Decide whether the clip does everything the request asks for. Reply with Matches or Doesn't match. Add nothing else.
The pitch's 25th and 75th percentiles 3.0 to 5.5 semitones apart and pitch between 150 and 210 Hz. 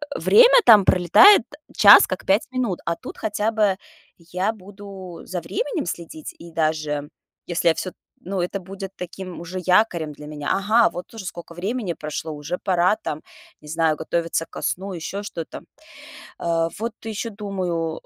Matches